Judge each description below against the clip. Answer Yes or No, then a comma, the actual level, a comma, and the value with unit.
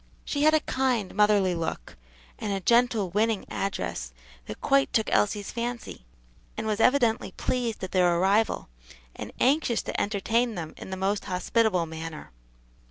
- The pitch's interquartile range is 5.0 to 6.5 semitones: No, average, 4.1 semitones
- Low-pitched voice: No, high, 210 Hz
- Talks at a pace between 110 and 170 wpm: Yes, average, 155 wpm